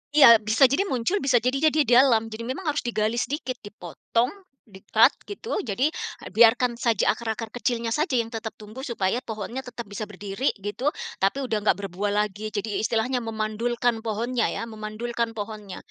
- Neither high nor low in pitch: No, high, 230 Hz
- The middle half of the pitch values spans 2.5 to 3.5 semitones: Yes, average, 2.8 semitones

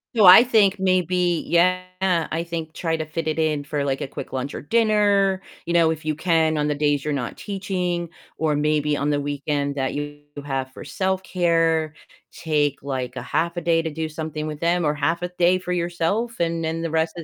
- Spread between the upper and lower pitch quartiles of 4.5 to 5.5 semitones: No, average, 3.2 semitones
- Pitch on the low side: No, medium, 160 Hz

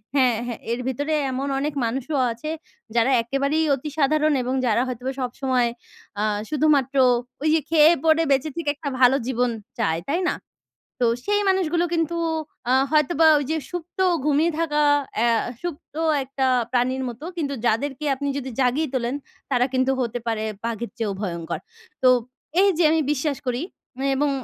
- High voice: Yes, very high, 275 Hz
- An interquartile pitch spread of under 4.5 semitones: Yes, average, 3.8 semitones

